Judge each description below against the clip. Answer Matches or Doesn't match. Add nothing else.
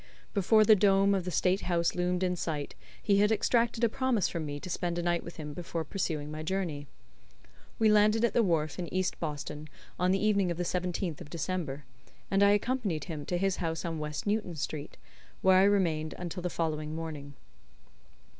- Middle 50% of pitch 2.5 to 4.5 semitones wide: Matches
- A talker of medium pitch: Matches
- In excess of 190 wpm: Matches